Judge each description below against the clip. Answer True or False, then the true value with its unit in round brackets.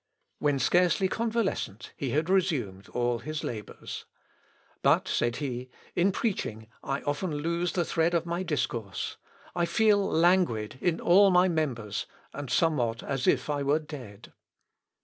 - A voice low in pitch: False (150 Hz)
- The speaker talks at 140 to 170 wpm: True (145 wpm)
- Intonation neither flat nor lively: False (6.4 semitones)